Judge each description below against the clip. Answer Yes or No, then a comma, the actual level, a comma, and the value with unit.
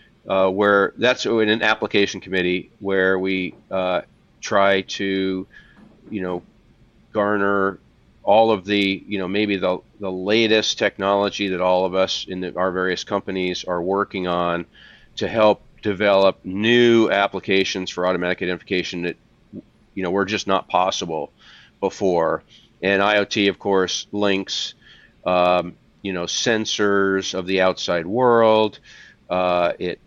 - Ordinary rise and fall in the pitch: No, narrow, 1.9 semitones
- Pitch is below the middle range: Yes, very low, 95 Hz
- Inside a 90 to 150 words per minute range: Yes, slow, 135 wpm